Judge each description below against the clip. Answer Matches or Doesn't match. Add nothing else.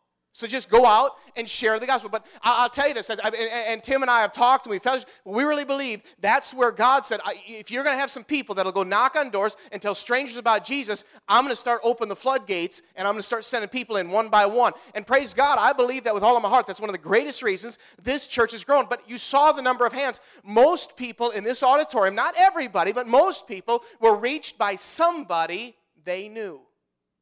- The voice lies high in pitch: Matches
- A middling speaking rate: Doesn't match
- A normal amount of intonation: Matches